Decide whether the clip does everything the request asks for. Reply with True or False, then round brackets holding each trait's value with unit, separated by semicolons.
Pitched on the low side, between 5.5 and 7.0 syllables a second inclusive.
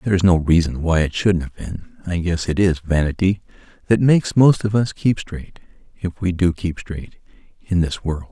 False (90 Hz; 5.1 syllables/s)